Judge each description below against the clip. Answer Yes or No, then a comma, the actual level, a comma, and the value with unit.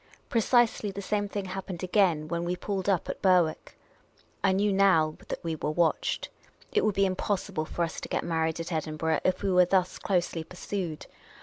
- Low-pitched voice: No, medium, 180 Hz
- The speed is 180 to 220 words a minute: Yes, average, 190 wpm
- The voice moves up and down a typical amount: Yes, average, 3.2 semitones